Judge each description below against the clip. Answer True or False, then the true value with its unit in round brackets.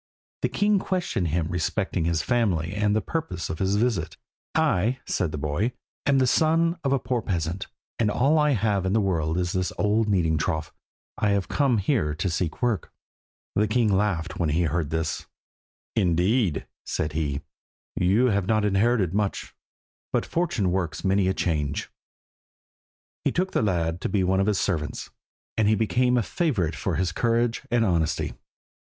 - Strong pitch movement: True (5.7 semitones)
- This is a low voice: True (100 Hz)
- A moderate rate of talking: True (175 wpm)